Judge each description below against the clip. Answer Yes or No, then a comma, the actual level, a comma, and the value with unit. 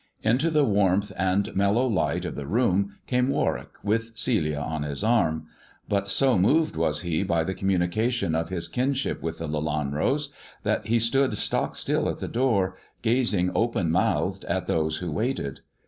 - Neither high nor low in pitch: No, low, 100 Hz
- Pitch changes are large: Yes, wide, 6.2 semitones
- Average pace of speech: Yes, average, 170 wpm